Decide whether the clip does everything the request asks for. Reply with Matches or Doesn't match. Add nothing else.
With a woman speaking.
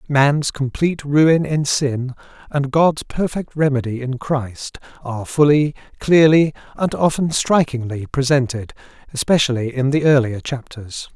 Doesn't match